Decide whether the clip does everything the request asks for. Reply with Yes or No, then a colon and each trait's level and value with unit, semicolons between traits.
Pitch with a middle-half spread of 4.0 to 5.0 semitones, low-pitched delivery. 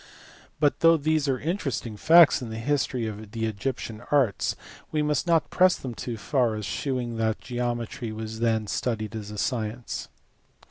Yes: average, 4.5 semitones; low, 120 Hz